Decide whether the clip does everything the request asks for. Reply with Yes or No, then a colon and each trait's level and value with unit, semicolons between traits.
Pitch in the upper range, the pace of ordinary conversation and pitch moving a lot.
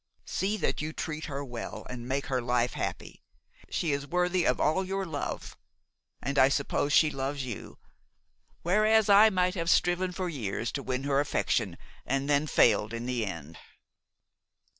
No: medium, 145 Hz; average, 165 wpm; wide, 5.9 semitones